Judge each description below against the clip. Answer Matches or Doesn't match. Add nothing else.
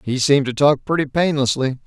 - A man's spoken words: Matches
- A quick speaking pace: Doesn't match